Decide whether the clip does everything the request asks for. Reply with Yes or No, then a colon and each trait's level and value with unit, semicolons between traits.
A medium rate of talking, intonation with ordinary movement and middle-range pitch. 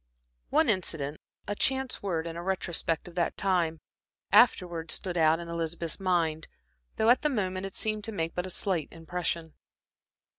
Yes: average, 165 wpm; average, 3.0 semitones; medium, 175 Hz